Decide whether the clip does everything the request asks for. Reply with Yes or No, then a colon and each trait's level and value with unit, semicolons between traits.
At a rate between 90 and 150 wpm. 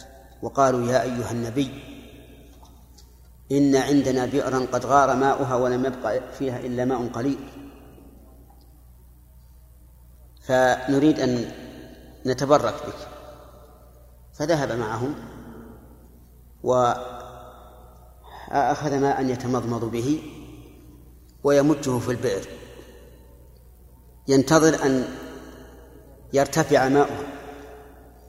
No: average, 70 wpm